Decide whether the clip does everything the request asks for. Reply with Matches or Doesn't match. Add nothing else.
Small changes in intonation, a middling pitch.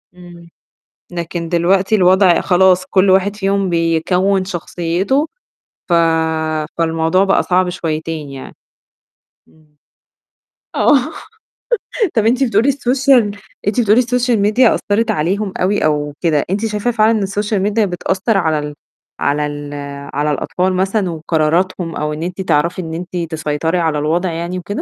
Doesn't match